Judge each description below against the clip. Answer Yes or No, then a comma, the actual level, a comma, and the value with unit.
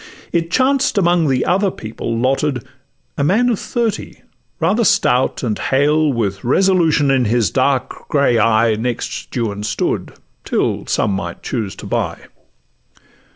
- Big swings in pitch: Yes, wide, 7.0 semitones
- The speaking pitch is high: No, low, 135 Hz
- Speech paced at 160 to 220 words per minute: No, average, 140 wpm